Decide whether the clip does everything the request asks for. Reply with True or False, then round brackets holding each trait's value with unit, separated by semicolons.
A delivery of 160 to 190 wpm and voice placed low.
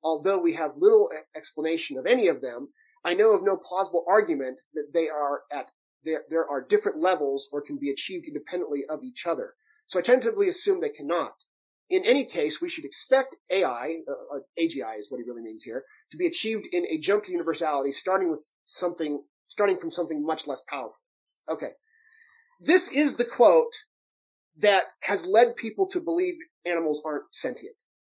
False (175 wpm; 190 Hz)